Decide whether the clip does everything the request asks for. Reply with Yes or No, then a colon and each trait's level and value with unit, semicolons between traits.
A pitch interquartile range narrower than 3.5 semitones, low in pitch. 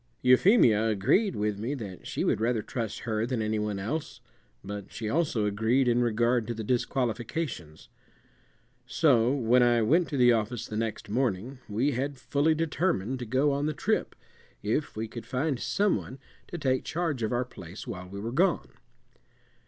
No: average, 4.3 semitones; low, 120 Hz